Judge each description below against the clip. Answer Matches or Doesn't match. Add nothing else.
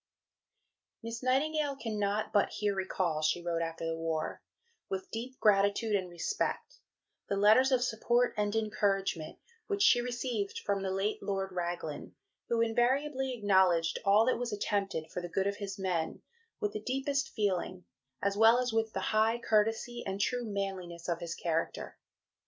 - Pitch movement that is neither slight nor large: Matches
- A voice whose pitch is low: Doesn't match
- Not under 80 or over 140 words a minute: Doesn't match